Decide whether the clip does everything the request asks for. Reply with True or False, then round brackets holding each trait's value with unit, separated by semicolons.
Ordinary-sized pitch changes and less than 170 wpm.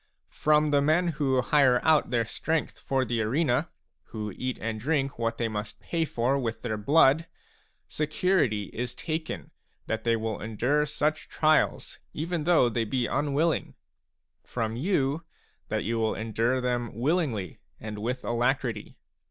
True (4.9 semitones; 150 wpm)